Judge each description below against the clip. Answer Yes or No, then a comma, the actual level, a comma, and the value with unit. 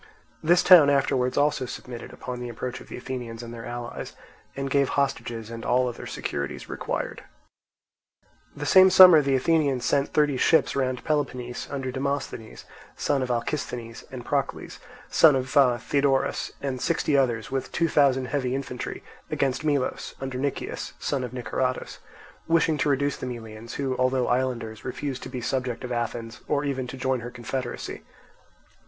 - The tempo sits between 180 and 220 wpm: No, average, 160 wpm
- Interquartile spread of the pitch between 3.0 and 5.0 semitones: No, narrow, 2.5 semitones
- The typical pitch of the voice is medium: No, low, 130 Hz